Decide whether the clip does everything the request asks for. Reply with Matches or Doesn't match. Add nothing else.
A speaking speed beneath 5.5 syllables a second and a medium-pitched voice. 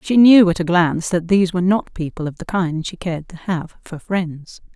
Matches